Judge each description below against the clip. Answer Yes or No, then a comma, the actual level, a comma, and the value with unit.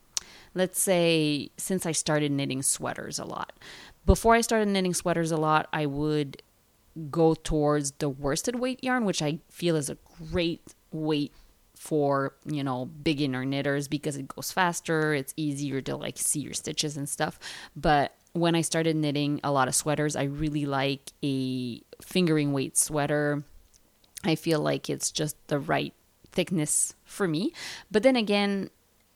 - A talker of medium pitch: Yes, medium, 150 Hz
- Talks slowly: No, average, 160 wpm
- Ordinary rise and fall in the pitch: Yes, average, 3.1 semitones